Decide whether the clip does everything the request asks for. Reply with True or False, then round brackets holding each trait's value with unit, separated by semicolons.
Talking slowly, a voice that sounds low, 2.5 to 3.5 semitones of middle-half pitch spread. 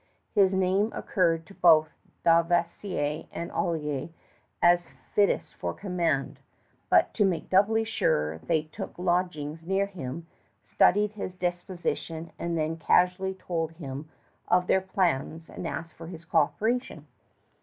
False (125 wpm; 175 Hz; 2.8 semitones)